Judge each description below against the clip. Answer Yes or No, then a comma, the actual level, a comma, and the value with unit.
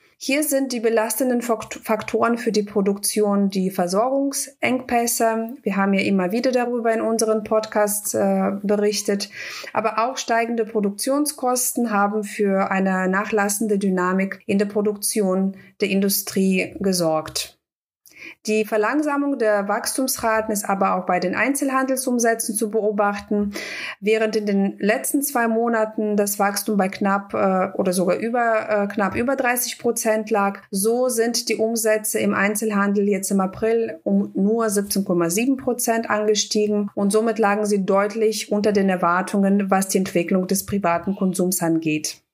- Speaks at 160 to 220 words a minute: No, average, 135 wpm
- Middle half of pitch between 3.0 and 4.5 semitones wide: No, narrow, 2.5 semitones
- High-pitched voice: Yes, high, 210 Hz